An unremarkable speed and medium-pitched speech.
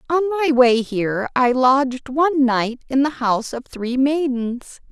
No: average, 170 wpm; very high, 260 Hz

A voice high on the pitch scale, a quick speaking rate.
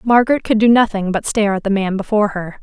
Yes: high, 210 Hz; fast, 250 wpm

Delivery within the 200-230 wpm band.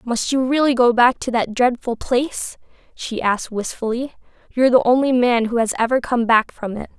Yes: fast, 205 wpm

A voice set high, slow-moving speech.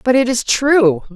No: high, 240 Hz; fast, 210 wpm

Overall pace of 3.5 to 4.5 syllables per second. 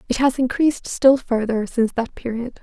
No: 5.3 syllables/s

